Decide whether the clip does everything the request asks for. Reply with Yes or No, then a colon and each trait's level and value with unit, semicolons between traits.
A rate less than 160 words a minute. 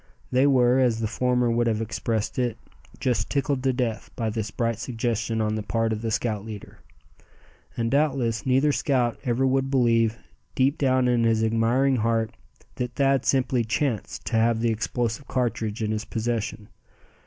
No: average, 170 wpm